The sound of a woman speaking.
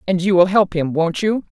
Yes: female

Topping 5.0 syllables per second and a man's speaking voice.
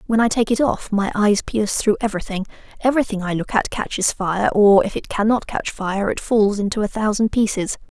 No: 5.6 syllables/s; female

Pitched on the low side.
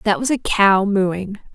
No: high, 200 Hz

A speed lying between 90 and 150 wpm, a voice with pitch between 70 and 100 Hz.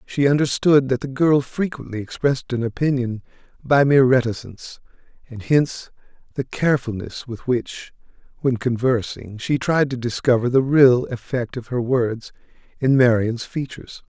No: average, 140 wpm; low, 125 Hz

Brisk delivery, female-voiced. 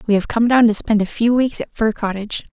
Yes: fast, 280 wpm; female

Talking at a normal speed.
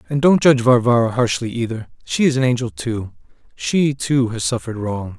Yes: average, 185 wpm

